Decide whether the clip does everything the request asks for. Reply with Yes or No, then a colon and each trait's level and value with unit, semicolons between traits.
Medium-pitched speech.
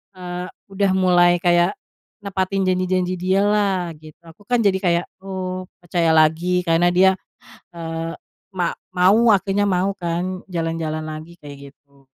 Yes: medium, 180 Hz